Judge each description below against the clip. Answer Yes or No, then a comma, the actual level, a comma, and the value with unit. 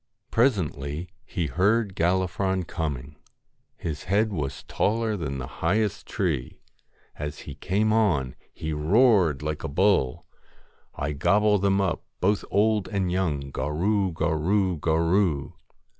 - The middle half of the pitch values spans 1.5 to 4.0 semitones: No, average, 5.3 semitones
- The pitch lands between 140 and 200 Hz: No, very low, 90 Hz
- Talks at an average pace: No, slow, 130 wpm